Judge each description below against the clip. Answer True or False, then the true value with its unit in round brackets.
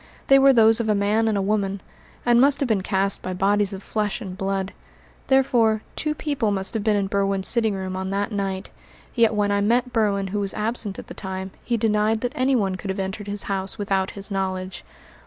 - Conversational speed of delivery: False (220 wpm)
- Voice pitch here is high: True (205 Hz)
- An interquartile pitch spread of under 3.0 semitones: True (2.6 semitones)